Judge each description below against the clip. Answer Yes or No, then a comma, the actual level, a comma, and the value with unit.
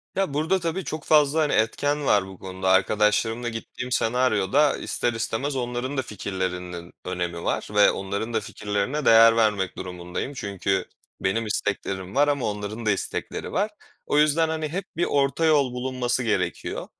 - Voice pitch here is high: No, low, 115 Hz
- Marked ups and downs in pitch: Yes, wide, 6.4 semitones